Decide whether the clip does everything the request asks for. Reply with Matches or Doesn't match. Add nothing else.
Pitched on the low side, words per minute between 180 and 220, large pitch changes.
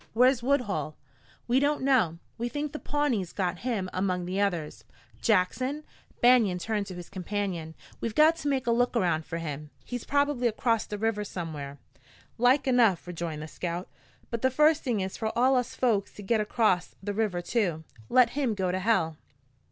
Doesn't match